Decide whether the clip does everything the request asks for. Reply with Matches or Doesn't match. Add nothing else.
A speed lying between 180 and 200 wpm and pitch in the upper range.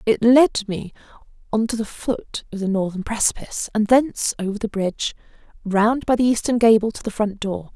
Matches